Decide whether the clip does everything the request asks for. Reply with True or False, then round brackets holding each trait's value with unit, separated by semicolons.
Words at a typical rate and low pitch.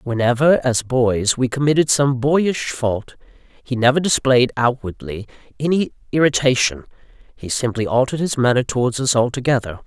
False (130 wpm; 125 Hz)